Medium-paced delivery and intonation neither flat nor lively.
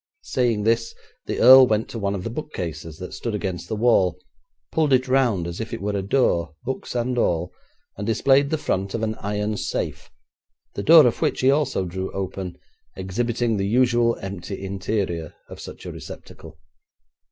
Yes: average, 180 wpm; average, 4.3 semitones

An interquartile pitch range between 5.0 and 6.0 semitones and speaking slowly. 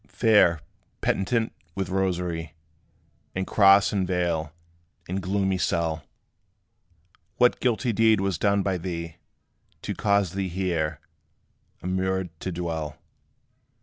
No: average, 2.7 semitones; slow, 110 wpm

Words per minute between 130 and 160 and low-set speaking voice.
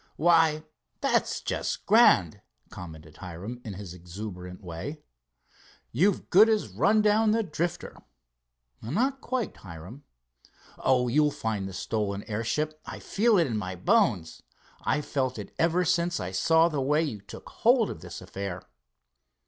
Yes: average, 145 wpm; low, 130 Hz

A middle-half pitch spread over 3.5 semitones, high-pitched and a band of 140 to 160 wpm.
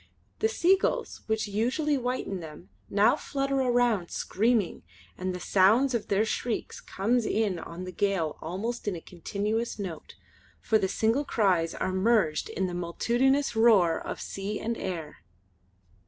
Yes: average, 4.6 semitones; high, 210 Hz; average, 150 wpm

